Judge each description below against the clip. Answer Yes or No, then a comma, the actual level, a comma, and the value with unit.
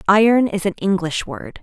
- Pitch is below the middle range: No, high, 190 Hz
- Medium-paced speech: Yes, average, 185 wpm